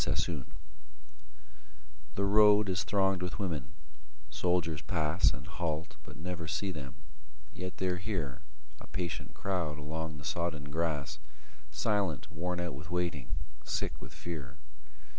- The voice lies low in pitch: Yes, very low, 85 Hz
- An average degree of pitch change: Yes, average, 3.3 semitones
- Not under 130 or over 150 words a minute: Yes, average, 140 wpm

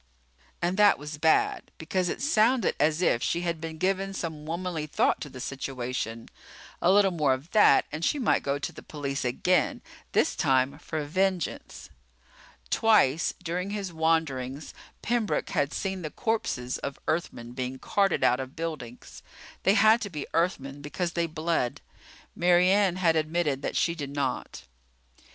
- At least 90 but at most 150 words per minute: No, average, 160 wpm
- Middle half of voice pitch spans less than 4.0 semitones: No, average, 4.9 semitones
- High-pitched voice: No, medium, 160 Hz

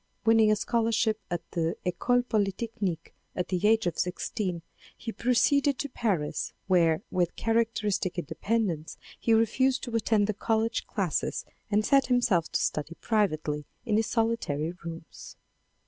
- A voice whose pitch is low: No, high, 215 Hz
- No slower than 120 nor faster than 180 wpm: Yes, average, 145 wpm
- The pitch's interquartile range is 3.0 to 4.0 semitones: No, average, 4.8 semitones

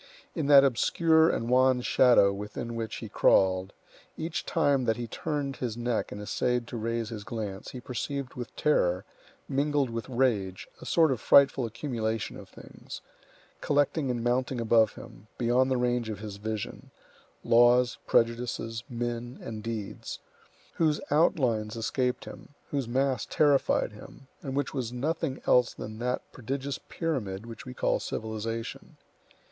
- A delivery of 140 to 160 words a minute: Yes, average, 145 wpm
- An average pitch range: Yes, average, 3.2 semitones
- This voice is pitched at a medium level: No, low, 120 Hz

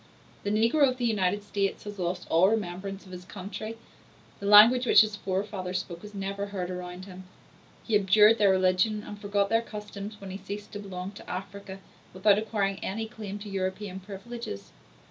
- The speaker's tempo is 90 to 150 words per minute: No, average, 185 wpm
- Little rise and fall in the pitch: Yes, narrow, 2.0 semitones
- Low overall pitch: No, high, 200 Hz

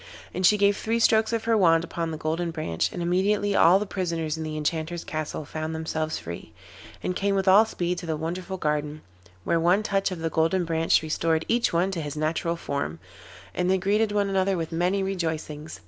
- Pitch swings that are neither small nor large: Yes, average, 3.5 semitones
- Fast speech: Yes, fast, 210 wpm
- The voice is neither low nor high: Yes, medium, 170 Hz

